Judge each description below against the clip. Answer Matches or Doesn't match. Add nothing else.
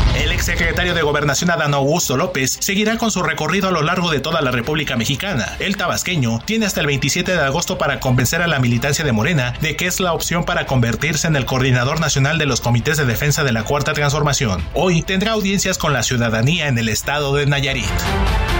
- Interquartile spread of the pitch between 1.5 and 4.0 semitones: Doesn't match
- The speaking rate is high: Matches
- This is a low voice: Doesn't match